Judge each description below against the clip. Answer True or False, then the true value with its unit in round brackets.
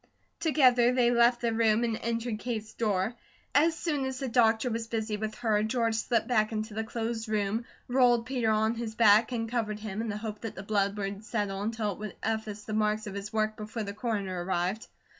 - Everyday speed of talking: False (215 wpm)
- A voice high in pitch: True (220 Hz)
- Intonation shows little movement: True (1.9 semitones)